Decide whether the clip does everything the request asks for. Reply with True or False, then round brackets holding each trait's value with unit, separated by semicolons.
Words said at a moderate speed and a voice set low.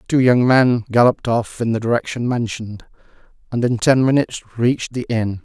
True (190 wpm; 120 Hz)